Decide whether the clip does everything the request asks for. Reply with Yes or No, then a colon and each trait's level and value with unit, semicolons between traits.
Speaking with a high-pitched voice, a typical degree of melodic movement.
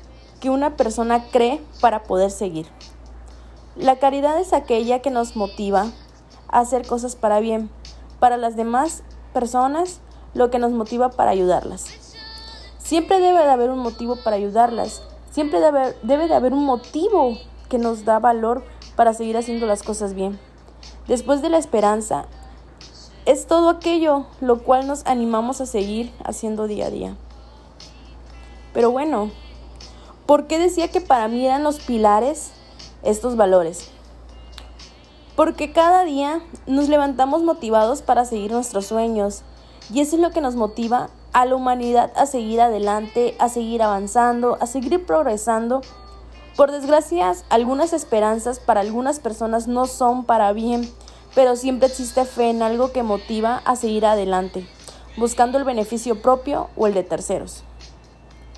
Yes: high, 235 Hz; average, 4.0 semitones